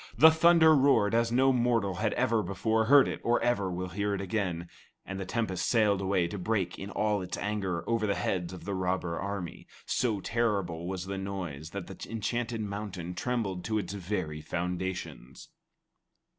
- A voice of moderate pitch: No, low, 100 Hz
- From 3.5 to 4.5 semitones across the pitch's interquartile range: Yes, average, 3.8 semitones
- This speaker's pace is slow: No, average, 180 wpm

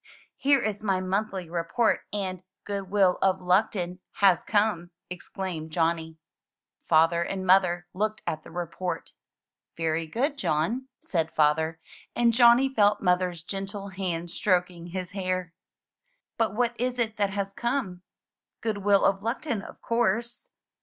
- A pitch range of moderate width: Yes, average, 3.6 semitones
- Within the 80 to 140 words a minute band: Yes, slow, 135 wpm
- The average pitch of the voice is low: No, high, 190 Hz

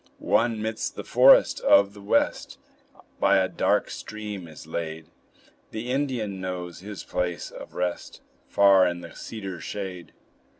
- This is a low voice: Yes, very low, 95 Hz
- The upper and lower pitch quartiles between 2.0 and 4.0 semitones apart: Yes, average, 3.5 semitones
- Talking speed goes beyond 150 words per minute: No, average, 140 wpm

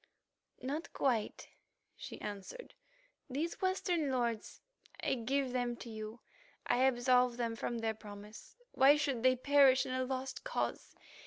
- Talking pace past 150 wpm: No, average, 140 wpm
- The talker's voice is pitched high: Yes, very high, 255 Hz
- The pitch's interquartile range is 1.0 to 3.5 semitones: Yes, average, 2.9 semitones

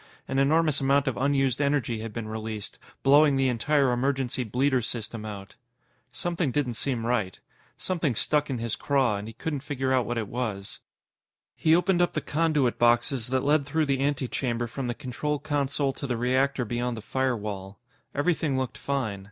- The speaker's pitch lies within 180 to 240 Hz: No, low, 130 Hz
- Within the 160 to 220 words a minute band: Yes, average, 175 wpm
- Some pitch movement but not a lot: Yes, average, 3.4 semitones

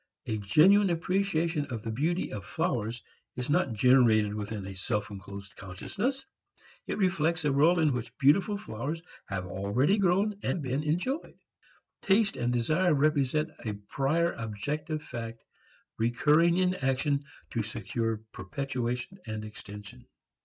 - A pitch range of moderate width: No, wide, 7.4 semitones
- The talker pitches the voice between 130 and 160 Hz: Yes, low, 135 Hz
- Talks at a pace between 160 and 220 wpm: No, slow, 135 wpm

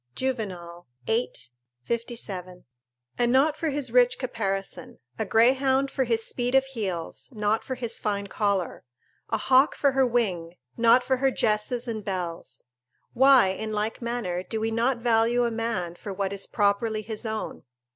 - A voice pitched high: Yes, high, 225 Hz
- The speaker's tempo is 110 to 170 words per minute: Yes, average, 160 wpm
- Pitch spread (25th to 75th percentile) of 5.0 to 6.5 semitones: No, average, 3.7 semitones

